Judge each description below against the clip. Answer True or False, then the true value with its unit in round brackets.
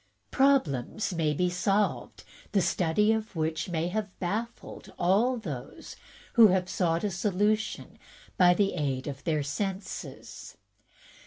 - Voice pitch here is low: False (185 Hz)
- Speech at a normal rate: False (120 wpm)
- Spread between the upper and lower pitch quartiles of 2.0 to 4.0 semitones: False (4.6 semitones)